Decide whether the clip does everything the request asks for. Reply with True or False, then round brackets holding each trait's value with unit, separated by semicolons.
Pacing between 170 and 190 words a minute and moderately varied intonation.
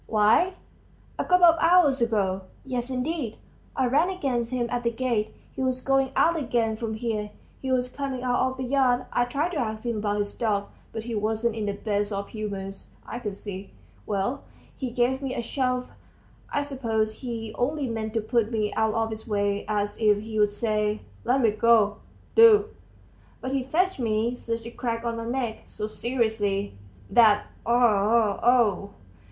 True (180 wpm; 3.3 semitones)